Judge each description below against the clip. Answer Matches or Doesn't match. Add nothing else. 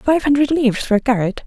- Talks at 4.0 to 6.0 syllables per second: Doesn't match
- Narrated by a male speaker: Doesn't match